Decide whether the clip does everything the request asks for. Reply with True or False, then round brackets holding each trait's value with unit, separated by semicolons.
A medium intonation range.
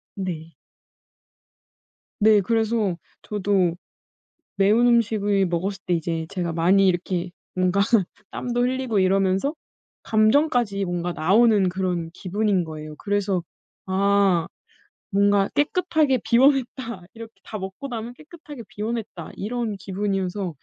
True (4.0 semitones)